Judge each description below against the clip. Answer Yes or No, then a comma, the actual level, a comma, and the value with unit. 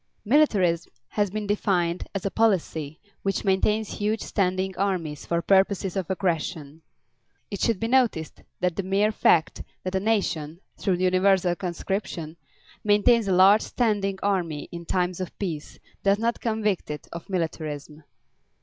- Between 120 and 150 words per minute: Yes, average, 145 wpm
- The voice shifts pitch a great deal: No, average, 3.3 semitones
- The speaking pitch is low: No, high, 190 Hz